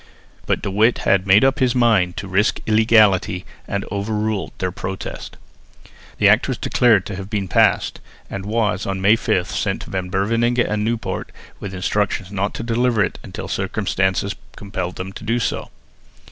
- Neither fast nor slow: Yes, average, 175 wpm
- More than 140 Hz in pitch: No, low, 100 Hz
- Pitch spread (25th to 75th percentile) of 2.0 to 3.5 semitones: Yes, narrow, 2.6 semitones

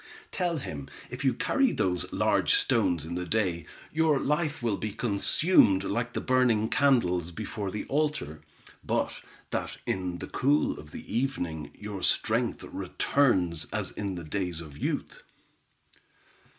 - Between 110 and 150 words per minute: Yes, average, 145 wpm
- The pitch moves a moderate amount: No, wide, 7.5 semitones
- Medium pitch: No, low, 105 Hz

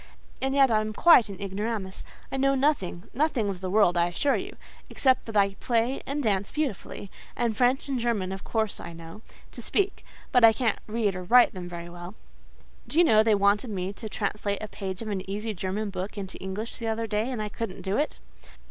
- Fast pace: Yes, fast, 210 wpm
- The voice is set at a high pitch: Yes, high, 215 Hz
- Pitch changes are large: No, average, 3.8 semitones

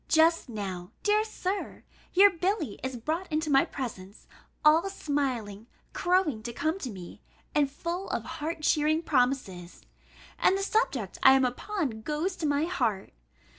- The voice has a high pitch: Yes, very high, 295 Hz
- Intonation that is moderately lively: No, wide, 6.7 semitones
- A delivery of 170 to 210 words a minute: No, average, 150 wpm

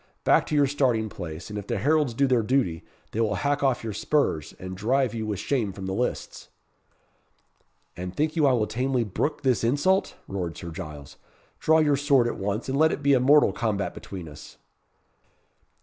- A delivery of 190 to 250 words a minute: Yes, average, 195 wpm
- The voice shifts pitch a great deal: Yes, wide, 6.2 semitones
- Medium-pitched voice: No, low, 120 Hz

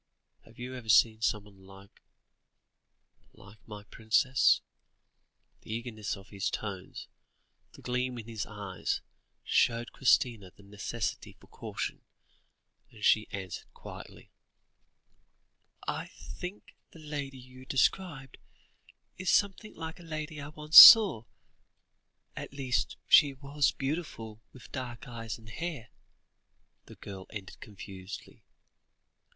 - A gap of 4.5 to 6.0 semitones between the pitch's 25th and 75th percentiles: Yes, average, 5.1 semitones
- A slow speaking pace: Yes, slow, 115 wpm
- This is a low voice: Yes, low, 120 Hz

